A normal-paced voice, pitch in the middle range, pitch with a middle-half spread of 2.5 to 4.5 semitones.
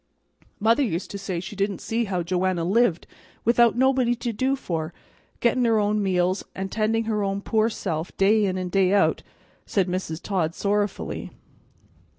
No: average, 170 wpm; high, 200 Hz; average, 3.6 semitones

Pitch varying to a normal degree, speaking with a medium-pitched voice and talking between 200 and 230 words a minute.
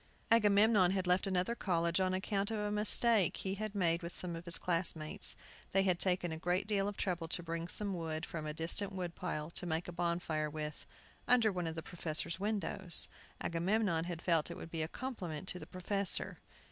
Yes: average, 3.0 semitones; medium, 180 Hz; fast, 205 wpm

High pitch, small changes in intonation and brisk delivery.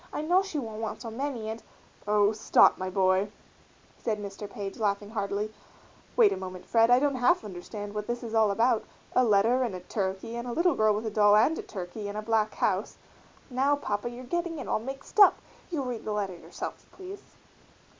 No: high, 220 Hz; average, 3.6 semitones; fast, 215 wpm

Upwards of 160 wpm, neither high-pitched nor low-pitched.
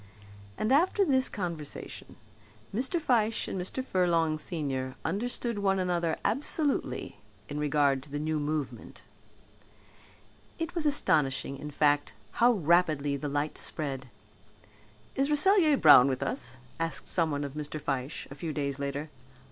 No: slow, 135 wpm; medium, 160 Hz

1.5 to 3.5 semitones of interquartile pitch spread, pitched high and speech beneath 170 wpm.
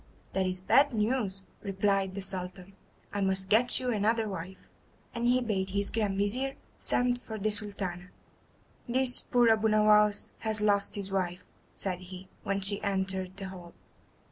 Yes: narrow, 2.5 semitones; high, 200 Hz; average, 160 wpm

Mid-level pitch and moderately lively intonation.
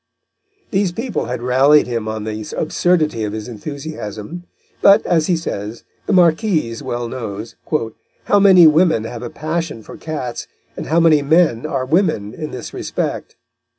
No: medium, 150 Hz; wide, 6.5 semitones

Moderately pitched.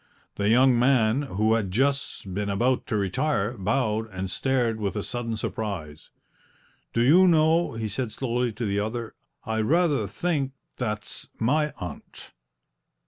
No: low, 115 Hz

